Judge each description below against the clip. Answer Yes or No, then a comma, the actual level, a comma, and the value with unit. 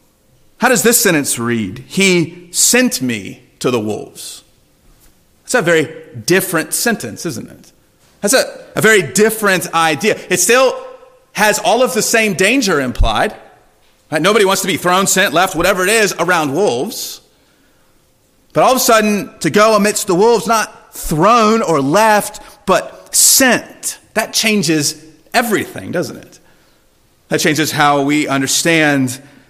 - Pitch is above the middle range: Yes, high, 195 Hz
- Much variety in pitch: Yes, wide, 5.8 semitones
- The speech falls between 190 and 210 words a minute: No, average, 145 wpm